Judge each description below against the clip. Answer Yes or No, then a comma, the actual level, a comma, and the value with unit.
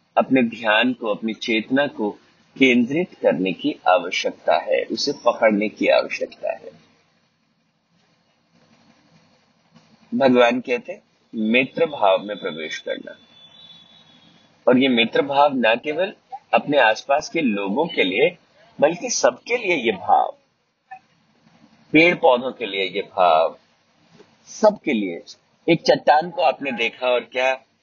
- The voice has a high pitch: No, medium, 140 Hz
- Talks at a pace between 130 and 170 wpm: No, average, 120 wpm